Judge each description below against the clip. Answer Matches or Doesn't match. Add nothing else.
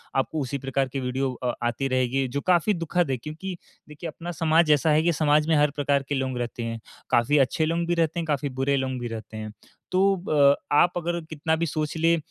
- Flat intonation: Doesn't match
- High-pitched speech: Doesn't match